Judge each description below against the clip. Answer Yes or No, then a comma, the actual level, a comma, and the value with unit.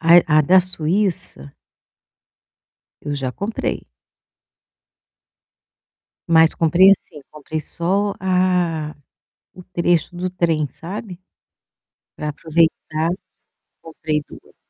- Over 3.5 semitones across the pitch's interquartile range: No, average, 3.0 semitones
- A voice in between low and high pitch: Yes, medium, 170 Hz